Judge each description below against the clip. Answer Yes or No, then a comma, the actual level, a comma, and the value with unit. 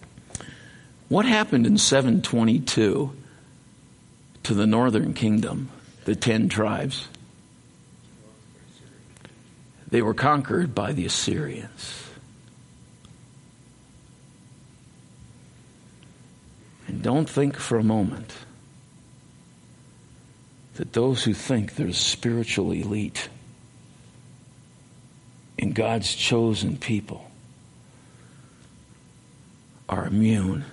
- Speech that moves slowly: Yes, slow, 70 wpm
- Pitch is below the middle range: Yes, low, 110 Hz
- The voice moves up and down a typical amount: Yes, average, 4.6 semitones